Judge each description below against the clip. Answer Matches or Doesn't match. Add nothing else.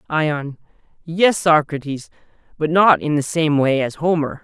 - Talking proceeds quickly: Doesn't match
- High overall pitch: Doesn't match